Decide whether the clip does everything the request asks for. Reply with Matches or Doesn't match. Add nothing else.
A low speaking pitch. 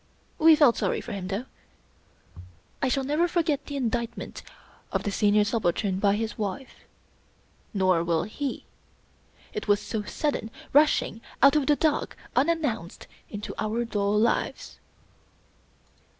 Doesn't match